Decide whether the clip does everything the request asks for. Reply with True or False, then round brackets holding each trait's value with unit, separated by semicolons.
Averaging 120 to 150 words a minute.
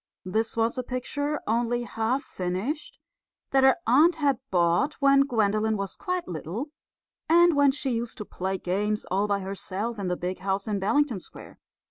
False (170 wpm)